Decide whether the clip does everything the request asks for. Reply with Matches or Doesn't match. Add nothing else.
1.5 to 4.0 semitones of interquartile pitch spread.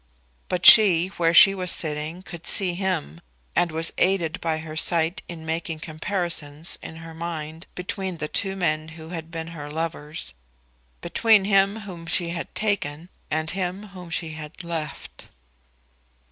Matches